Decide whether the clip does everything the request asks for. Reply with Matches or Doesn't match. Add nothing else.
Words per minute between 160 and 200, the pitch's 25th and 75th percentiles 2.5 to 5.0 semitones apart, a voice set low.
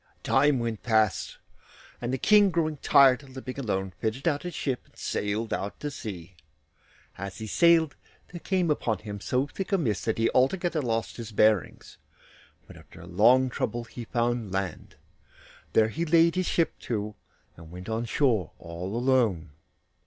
Doesn't match